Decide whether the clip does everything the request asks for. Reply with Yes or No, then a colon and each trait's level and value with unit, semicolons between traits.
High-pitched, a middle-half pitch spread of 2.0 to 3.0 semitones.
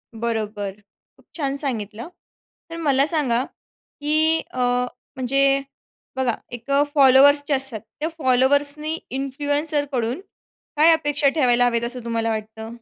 No: very high, 265 Hz; average, 3.8 semitones